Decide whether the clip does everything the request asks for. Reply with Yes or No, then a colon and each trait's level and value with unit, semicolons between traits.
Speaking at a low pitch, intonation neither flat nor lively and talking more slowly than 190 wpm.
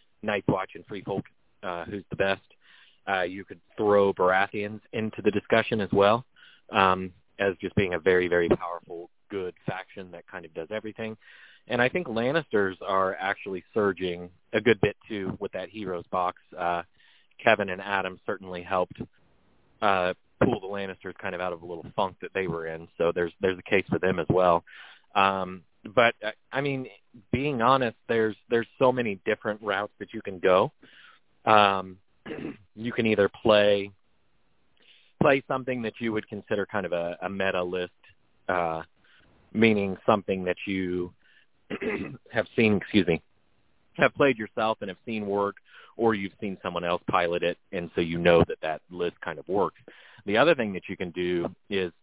Yes: very low, 95 Hz; average, 3.1 semitones; average, 175 wpm